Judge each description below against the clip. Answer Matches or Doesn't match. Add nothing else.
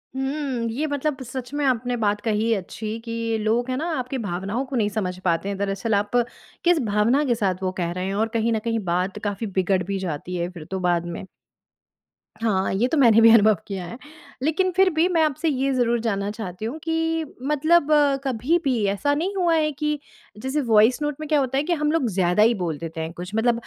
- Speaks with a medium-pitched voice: Doesn't match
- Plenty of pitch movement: Matches